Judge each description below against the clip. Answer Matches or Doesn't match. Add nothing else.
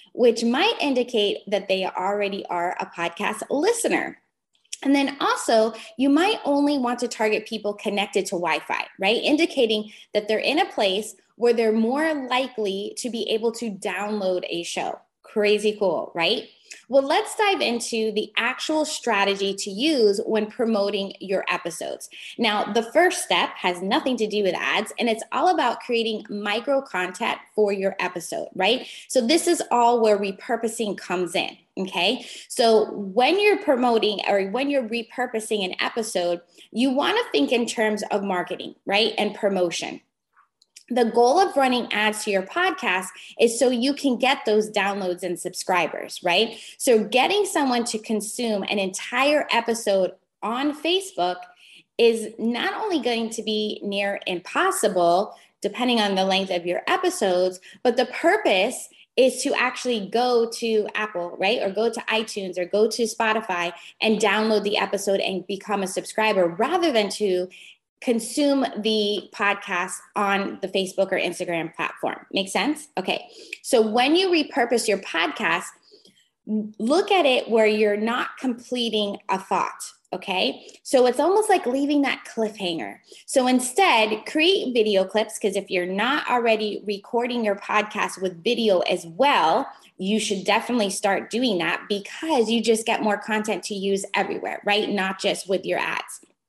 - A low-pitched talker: Doesn't match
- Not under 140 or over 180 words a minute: Matches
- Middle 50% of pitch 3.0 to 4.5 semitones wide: Matches